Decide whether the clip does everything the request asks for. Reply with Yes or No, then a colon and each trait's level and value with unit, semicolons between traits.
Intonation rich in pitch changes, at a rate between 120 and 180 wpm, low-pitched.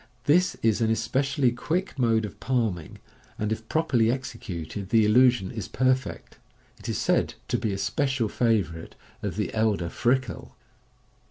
No: average, 3.7 semitones; average, 150 wpm; low, 115 Hz